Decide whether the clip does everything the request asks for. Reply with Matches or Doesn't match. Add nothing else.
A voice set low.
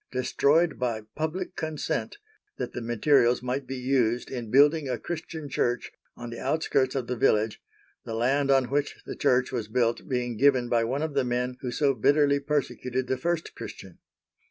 Matches